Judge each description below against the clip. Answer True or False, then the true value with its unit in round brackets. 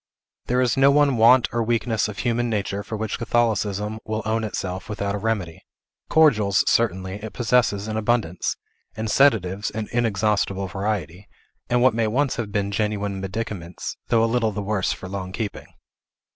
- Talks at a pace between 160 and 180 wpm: True (170 wpm)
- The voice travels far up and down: False (2.7 semitones)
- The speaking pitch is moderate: False (110 Hz)